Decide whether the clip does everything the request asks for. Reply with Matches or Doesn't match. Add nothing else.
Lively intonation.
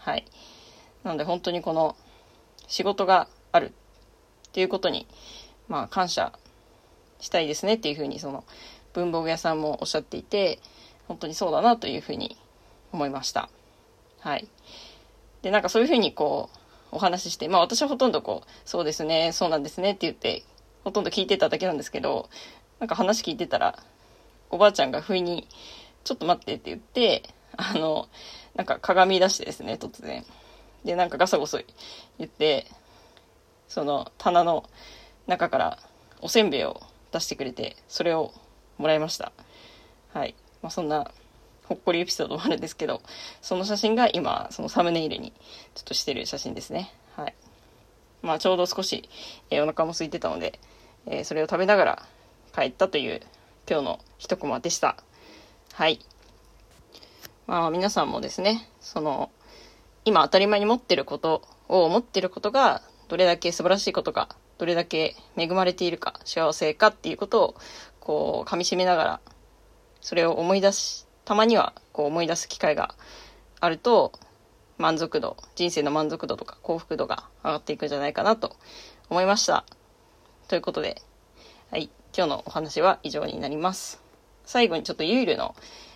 Doesn't match